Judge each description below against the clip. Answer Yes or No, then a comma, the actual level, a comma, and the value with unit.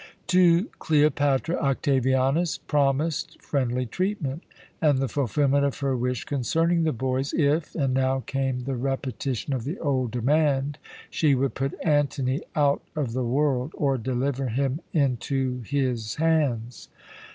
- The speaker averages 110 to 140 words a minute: Yes, slow, 135 wpm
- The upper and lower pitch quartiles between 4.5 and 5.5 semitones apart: No, narrow, 2.5 semitones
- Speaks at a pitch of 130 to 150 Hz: Yes, low, 135 Hz